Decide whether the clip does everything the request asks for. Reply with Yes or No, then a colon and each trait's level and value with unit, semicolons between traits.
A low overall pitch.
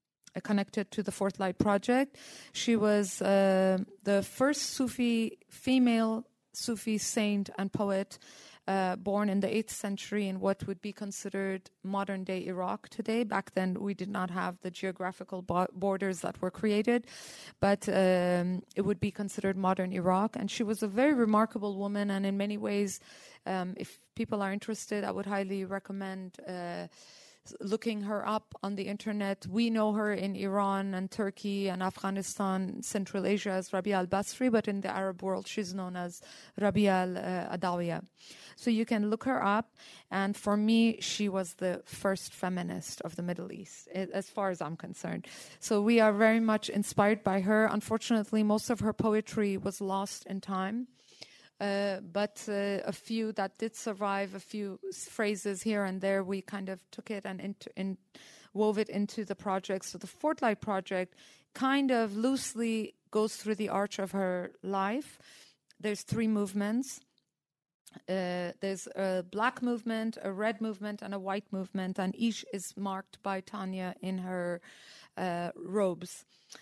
No: high, 200 Hz